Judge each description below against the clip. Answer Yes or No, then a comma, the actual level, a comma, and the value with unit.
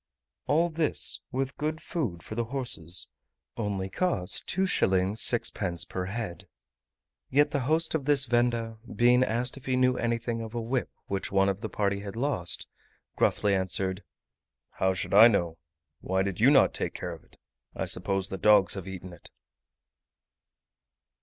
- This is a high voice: No, low, 110 Hz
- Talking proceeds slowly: No, average, 160 wpm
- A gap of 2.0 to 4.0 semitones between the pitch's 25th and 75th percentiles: No, average, 5.1 semitones